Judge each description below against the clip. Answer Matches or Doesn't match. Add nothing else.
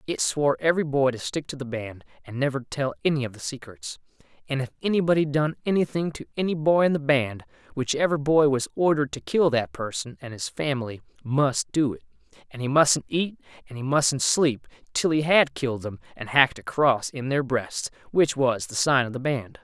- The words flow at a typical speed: Doesn't match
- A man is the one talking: Matches